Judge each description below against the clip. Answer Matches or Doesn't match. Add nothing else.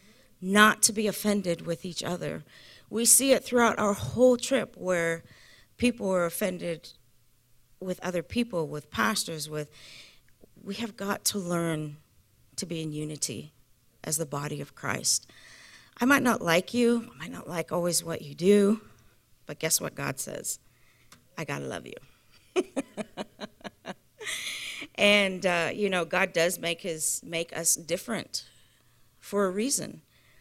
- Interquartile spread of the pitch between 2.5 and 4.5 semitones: Doesn't match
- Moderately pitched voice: Matches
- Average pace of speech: Matches